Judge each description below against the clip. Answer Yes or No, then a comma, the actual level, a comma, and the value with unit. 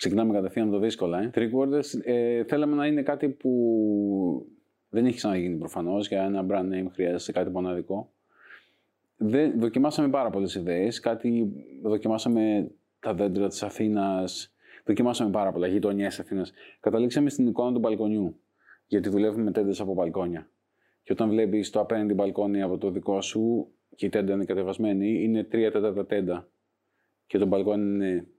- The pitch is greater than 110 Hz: No, low, 105 Hz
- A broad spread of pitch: No, narrow, 2.6 semitones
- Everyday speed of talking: Yes, average, 155 wpm